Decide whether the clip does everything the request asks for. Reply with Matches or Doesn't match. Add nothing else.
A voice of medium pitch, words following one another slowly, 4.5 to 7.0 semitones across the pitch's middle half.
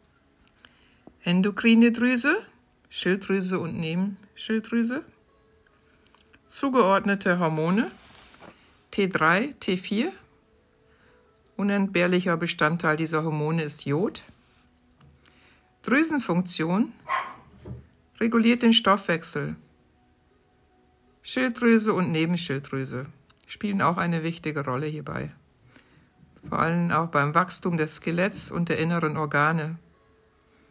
Matches